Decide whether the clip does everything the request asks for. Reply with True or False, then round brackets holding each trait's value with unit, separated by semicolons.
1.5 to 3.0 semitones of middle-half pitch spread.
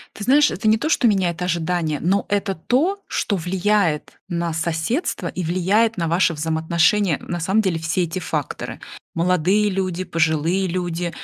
False (3.4 semitones)